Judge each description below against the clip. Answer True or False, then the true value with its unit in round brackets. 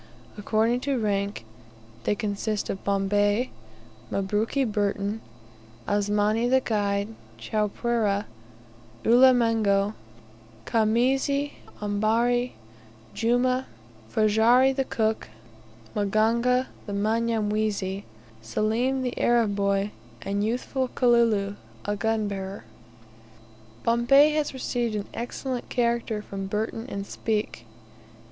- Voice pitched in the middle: False (220 Hz)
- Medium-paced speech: False (90 wpm)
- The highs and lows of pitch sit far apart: False (2.9 semitones)